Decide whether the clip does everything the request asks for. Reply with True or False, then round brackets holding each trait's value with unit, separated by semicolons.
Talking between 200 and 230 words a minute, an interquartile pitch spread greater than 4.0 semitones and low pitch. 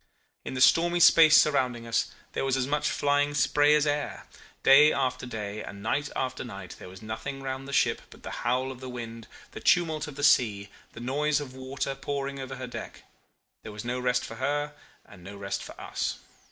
False (205 wpm; 3.5 semitones; 130 Hz)